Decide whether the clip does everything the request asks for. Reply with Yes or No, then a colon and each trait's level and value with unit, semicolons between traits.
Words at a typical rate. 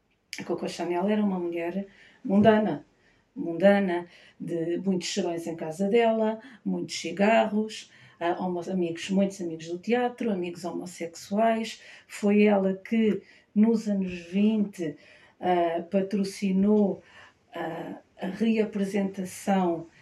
No: slow, 110 wpm